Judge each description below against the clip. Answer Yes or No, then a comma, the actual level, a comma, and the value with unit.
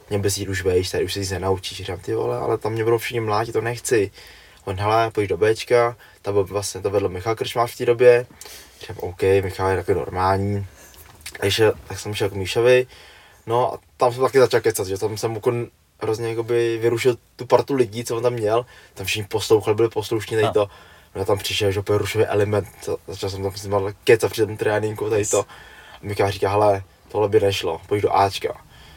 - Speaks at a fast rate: Yes, fast, 205 wpm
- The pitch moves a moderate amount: Yes, average, 3.3 semitones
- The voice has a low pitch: Yes, low, 105 Hz